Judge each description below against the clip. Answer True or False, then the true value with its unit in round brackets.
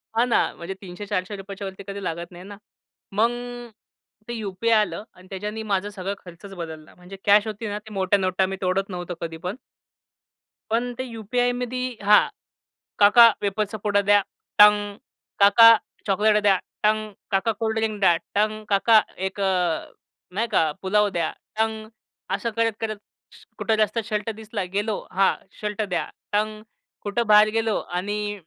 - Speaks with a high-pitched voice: True (205 Hz)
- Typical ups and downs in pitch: False (2.1 semitones)